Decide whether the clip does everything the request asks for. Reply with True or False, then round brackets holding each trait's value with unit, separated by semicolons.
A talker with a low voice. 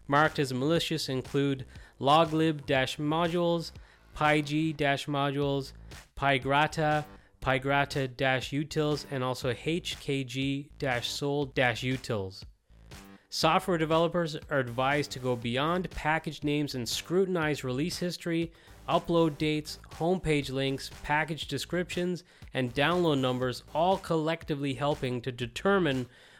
False (145 Hz)